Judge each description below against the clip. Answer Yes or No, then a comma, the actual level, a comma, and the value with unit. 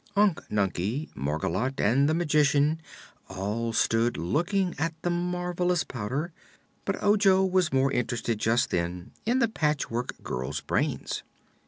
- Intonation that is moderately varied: No, wide, 7.8 semitones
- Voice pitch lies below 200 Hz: Yes, medium, 140 Hz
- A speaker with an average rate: No, slow, 130 wpm